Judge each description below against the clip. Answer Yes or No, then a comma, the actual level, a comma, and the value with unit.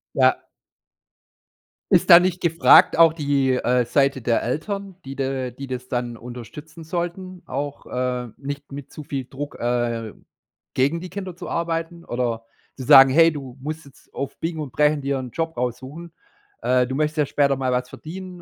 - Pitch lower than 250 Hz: Yes, medium, 140 Hz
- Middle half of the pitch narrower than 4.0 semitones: No, average, 4.4 semitones